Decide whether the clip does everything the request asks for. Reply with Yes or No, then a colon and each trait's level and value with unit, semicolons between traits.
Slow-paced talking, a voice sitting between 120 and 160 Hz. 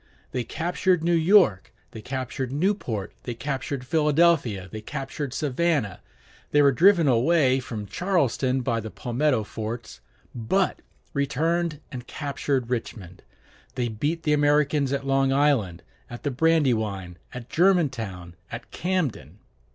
Yes: slow, 130 wpm; low, 135 Hz